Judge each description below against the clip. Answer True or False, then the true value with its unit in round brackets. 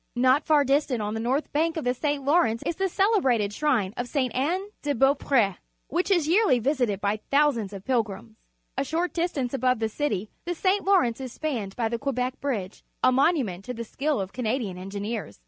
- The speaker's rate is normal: False (215 wpm)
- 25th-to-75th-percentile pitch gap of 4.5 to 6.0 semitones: True (5.1 semitones)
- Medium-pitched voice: False (255 Hz)